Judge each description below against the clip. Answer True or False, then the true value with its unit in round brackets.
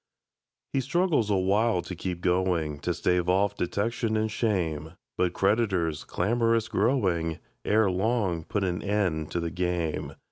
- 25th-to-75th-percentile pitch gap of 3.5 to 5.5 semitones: True (3.9 semitones)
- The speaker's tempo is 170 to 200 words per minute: False (140 wpm)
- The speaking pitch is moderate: False (95 Hz)